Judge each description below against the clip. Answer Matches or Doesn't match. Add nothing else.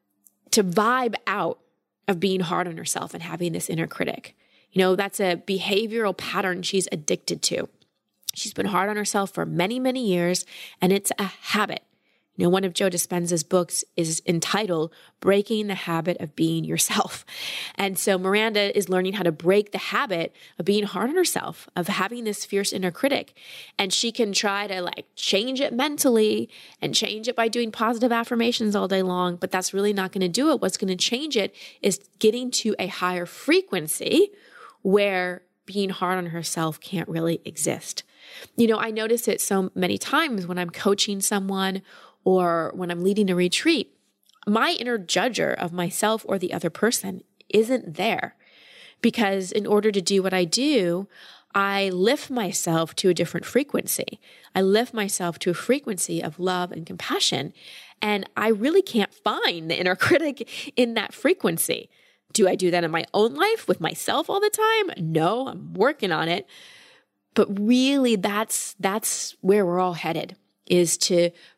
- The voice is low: Doesn't match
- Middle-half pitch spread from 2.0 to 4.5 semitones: Matches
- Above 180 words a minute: Doesn't match